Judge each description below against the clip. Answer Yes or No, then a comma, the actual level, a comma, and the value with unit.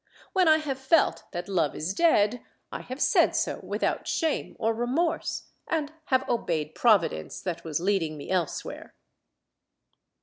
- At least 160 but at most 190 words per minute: No, average, 145 wpm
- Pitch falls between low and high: No, high, 220 Hz